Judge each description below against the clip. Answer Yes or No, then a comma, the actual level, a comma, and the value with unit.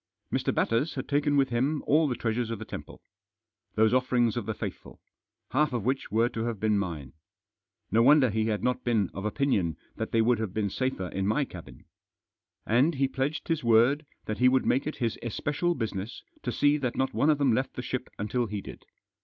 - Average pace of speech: No, fast, 215 wpm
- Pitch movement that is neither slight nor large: Yes, average, 3.8 semitones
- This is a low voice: Yes, low, 120 Hz